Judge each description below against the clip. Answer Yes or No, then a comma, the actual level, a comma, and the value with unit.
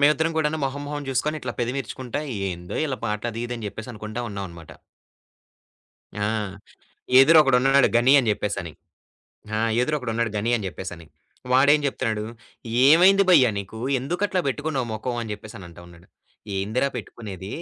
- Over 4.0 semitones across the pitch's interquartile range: Yes, average, 5.2 semitones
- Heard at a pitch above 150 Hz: No, low, 120 Hz